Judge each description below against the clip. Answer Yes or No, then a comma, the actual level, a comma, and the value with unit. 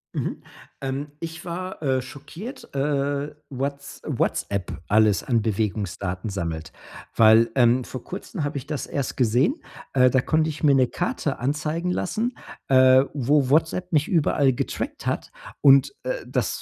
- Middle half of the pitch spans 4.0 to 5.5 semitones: Yes, average, 4.4 semitones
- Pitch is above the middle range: No, medium, 140 Hz